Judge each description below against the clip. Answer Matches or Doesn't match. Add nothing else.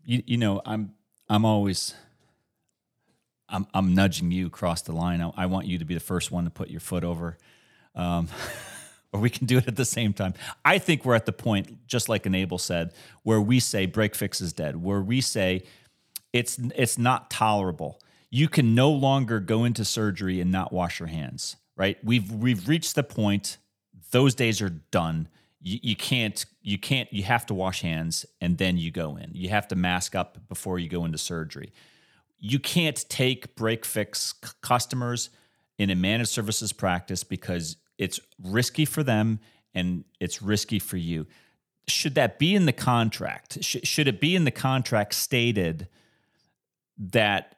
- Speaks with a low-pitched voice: Matches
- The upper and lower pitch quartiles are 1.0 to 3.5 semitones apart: Doesn't match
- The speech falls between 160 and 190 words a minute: Matches